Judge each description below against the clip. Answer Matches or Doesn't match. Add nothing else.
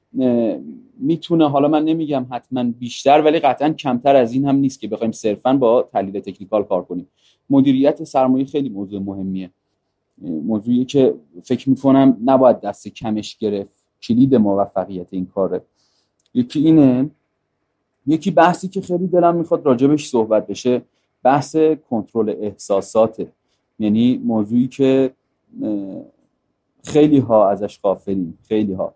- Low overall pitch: Matches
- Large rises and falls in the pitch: Matches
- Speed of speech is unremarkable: Matches